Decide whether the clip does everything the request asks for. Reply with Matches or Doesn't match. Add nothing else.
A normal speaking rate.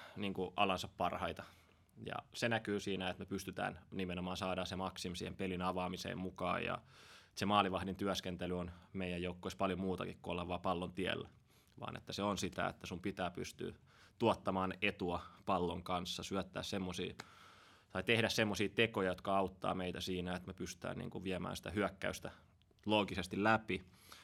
Doesn't match